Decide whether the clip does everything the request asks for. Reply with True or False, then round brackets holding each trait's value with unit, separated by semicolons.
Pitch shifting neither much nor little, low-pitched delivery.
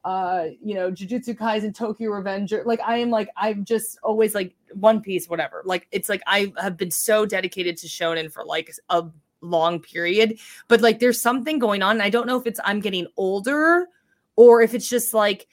False (3.9 semitones; 210 Hz)